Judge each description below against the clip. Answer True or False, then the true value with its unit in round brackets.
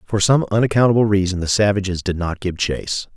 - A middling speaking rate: True (190 wpm)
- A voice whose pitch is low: True (100 Hz)